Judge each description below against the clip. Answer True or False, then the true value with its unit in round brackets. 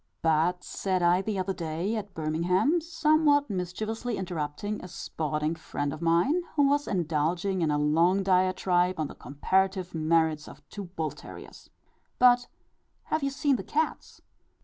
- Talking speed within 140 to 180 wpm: True (150 wpm)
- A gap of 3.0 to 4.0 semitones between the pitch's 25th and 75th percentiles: False (5.1 semitones)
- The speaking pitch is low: False (180 Hz)